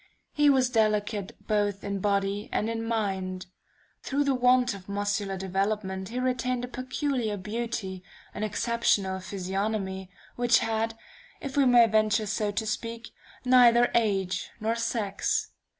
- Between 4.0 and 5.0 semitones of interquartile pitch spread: No, average, 3.2 semitones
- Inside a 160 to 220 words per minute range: No, slow, 135 wpm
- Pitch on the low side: No, high, 215 Hz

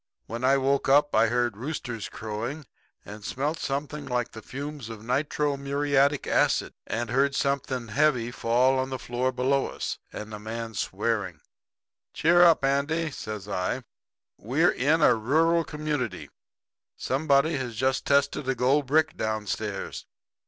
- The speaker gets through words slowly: No, average, 145 wpm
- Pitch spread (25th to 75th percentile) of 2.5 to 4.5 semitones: Yes, average, 3.8 semitones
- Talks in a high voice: No, low, 135 Hz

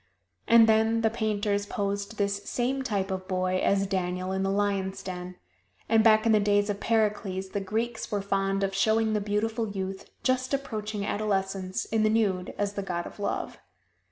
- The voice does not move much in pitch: Yes, narrow, 2.2 semitones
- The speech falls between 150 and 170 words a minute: No, average, 185 wpm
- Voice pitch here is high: Yes, high, 205 Hz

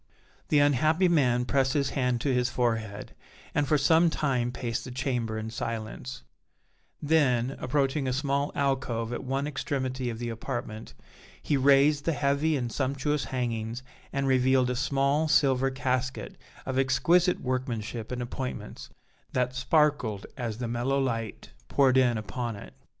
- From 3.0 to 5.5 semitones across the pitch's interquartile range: No, narrow, 2.6 semitones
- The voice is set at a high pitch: No, low, 130 Hz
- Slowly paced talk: No, average, 150 wpm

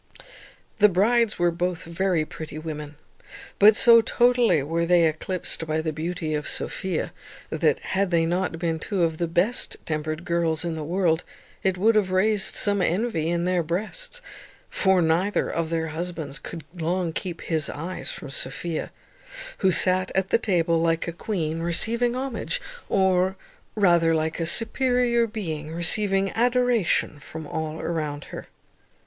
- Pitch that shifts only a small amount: No, average, 3.6 semitones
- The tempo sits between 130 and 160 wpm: Yes, average, 155 wpm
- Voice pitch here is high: No, medium, 175 Hz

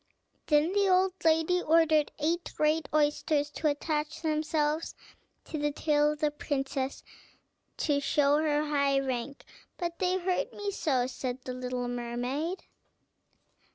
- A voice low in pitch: No, very high, 300 Hz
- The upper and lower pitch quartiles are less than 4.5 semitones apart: Yes, narrow, 2.6 semitones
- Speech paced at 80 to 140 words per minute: Yes, slow, 135 wpm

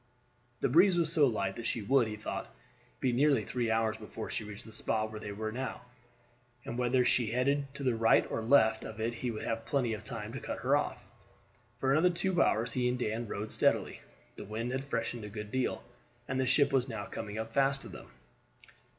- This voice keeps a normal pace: No, fast, 220 wpm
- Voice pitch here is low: Yes, low, 120 Hz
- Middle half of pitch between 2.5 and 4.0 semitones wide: Yes, average, 3.4 semitones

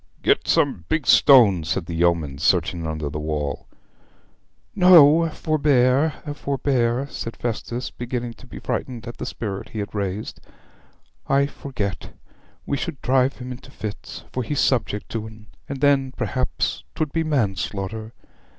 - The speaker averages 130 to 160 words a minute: Yes, average, 145 wpm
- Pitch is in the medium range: No, low, 120 Hz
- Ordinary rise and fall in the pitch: No, wide, 6.0 semitones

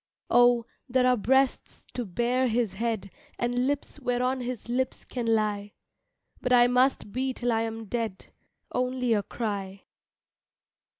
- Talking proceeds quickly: No, average, 140 wpm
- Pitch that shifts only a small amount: Yes, narrow, 2.1 semitones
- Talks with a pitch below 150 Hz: No, high, 240 Hz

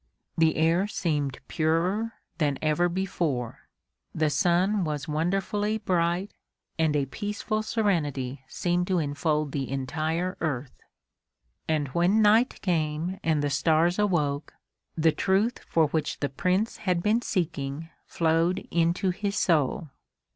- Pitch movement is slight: No, average, 4.0 semitones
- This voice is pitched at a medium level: Yes, medium, 165 Hz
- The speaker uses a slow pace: Yes, slow, 125 wpm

